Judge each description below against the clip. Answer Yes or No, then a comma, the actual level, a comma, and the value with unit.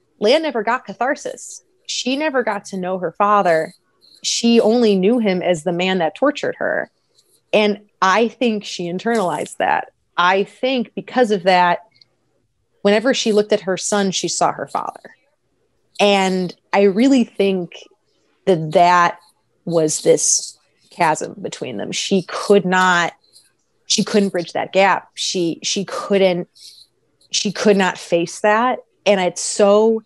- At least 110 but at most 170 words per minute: Yes, average, 145 wpm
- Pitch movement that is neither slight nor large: Yes, average, 3.5 semitones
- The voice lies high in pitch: Yes, high, 200 Hz